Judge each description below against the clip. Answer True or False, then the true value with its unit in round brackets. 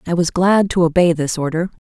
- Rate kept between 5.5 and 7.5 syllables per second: True (5.7 syllables/s)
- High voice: False (170 Hz)